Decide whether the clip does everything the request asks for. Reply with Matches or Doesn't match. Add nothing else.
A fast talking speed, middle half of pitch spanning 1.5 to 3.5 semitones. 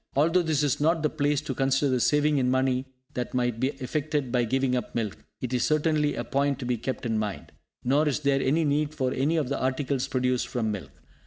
Matches